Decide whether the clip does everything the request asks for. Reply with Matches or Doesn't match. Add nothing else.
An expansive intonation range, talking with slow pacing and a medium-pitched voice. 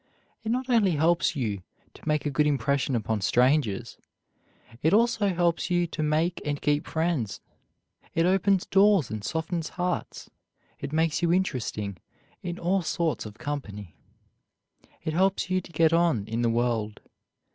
Doesn't match